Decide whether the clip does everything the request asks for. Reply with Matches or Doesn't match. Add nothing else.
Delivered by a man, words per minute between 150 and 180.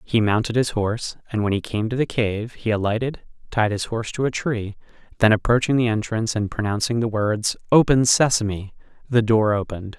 Doesn't match